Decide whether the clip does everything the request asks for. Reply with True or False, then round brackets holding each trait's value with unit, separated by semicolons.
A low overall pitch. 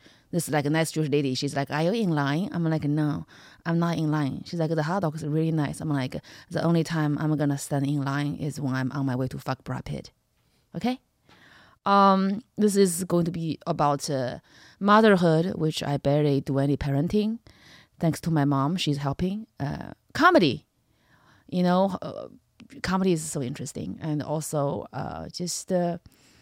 False (155 Hz)